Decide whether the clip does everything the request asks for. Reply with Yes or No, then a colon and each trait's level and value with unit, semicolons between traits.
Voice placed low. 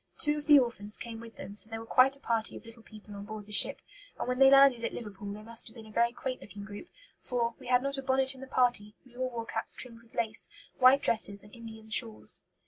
No: high, 230 Hz